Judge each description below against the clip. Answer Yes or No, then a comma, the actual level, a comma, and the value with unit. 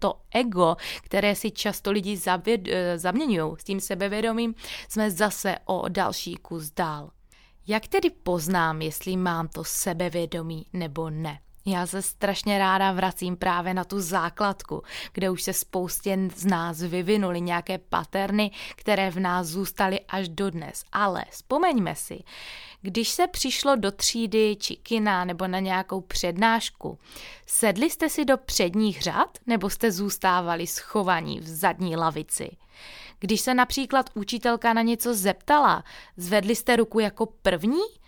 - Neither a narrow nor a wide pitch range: Yes, average, 3.5 semitones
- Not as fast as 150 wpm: Yes, average, 140 wpm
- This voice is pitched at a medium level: No, high, 195 Hz